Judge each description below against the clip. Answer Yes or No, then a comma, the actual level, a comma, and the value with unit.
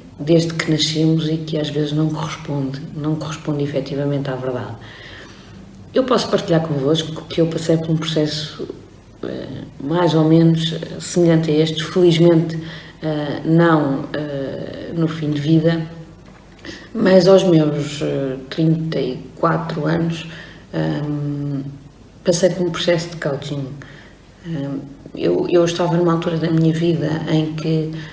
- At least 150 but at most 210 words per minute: No, slow, 120 wpm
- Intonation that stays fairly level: Yes, narrow, 2.2 semitones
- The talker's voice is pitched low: No, medium, 160 Hz